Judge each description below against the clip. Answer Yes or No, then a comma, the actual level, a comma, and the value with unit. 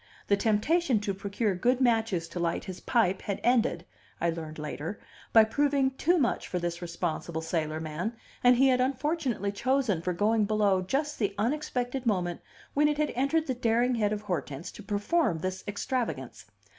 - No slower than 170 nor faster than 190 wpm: Yes, average, 175 wpm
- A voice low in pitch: No, high, 210 Hz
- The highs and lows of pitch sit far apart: Yes, wide, 6.2 semitones